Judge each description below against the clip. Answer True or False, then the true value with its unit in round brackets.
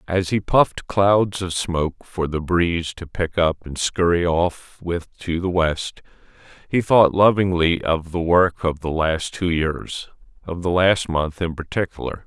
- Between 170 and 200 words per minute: True (175 wpm)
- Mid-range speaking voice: False (85 Hz)